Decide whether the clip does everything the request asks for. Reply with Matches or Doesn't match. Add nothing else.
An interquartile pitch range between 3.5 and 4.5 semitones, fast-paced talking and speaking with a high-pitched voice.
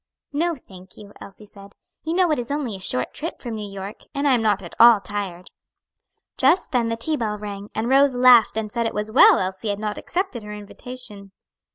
Matches